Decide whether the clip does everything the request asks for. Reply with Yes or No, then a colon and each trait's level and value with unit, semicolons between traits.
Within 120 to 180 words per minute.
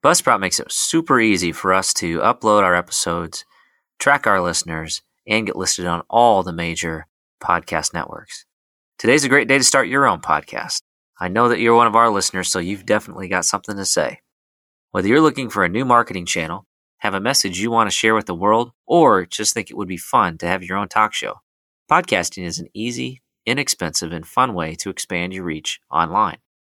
No: fast, 205 wpm